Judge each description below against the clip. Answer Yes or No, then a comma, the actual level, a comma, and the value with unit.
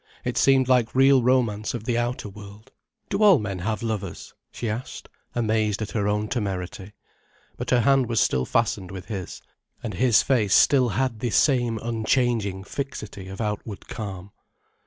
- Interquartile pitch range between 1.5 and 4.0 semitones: Yes, average, 3.5 semitones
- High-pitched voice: No, low, 110 Hz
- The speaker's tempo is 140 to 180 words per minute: Yes, average, 165 wpm